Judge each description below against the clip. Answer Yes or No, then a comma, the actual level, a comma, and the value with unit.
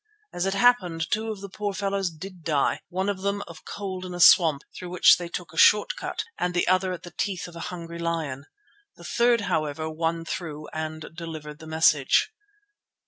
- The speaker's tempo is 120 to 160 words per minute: No, average, 200 wpm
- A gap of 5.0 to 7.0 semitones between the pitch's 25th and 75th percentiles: No, average, 3.3 semitones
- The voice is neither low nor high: Yes, medium, 175 Hz